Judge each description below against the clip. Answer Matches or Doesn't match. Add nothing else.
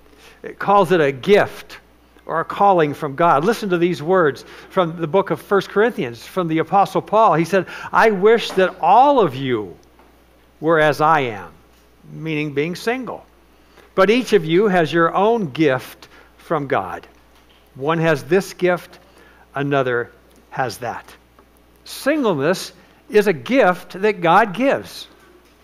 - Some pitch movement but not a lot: Doesn't match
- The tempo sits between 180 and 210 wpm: Doesn't match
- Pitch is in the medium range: Matches